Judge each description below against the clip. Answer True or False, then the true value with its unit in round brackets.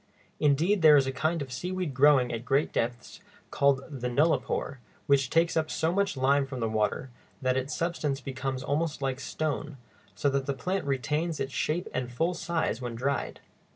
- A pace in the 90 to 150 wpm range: False (185 wpm)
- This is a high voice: False (140 Hz)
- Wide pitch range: False (3.5 semitones)